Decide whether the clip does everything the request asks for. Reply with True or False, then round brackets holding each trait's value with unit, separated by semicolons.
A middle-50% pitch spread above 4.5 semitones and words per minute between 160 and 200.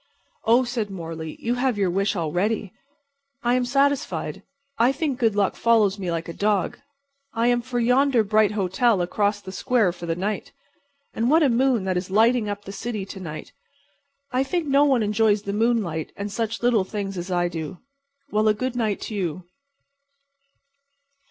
False (4.2 semitones; 180 wpm)